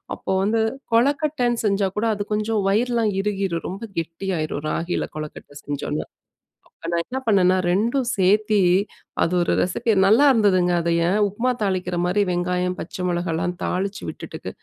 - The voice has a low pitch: No, high, 195 Hz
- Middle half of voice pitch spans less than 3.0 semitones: No, average, 3.5 semitones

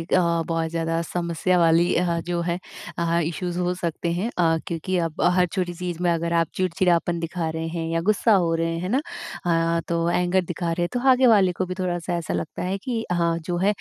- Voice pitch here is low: No, medium, 175 Hz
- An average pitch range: No, narrow, 1.5 semitones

